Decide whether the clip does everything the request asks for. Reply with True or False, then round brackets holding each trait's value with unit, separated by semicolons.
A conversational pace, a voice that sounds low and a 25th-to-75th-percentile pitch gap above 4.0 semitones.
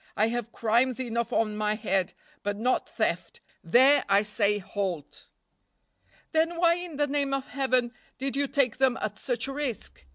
False (170 wpm; 240 Hz; 4.6 semitones)